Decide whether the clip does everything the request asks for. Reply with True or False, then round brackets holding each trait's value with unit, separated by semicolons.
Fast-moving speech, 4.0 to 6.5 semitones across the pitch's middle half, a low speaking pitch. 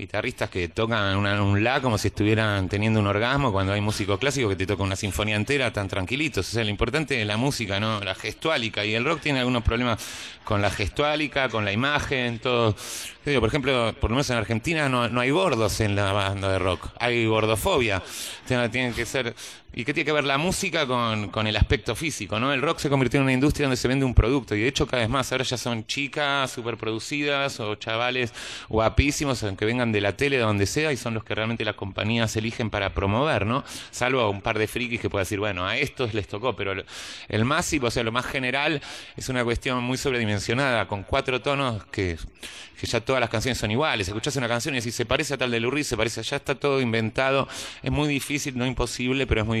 True (230 wpm; 4.3 semitones; 120 Hz)